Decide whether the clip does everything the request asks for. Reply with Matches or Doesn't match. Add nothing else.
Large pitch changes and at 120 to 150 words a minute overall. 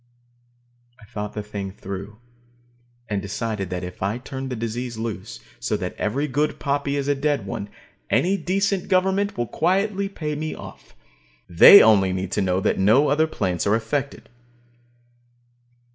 Doesn't match